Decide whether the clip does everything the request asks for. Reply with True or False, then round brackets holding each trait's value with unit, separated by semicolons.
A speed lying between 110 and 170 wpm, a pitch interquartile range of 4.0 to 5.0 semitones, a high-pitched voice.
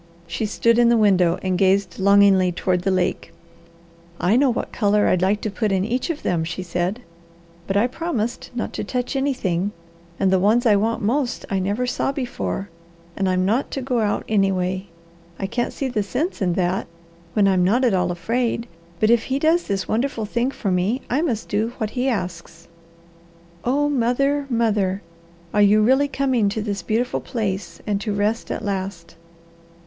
False (185 wpm; 4.4 semitones; 210 Hz)